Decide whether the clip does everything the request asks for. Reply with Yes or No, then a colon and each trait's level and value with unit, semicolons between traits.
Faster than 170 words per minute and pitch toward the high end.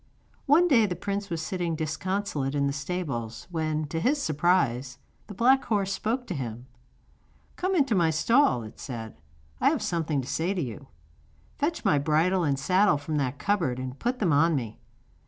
No: average, 180 wpm; medium, 165 Hz